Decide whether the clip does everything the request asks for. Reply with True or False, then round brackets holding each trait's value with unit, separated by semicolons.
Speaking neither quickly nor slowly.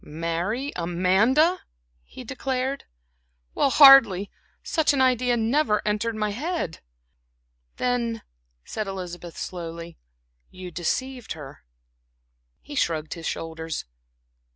False (100 wpm)